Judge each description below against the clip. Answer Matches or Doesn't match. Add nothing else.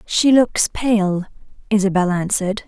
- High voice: Matches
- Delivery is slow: Matches